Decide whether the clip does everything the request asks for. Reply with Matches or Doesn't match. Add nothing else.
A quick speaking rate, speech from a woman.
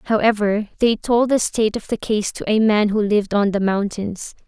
Matches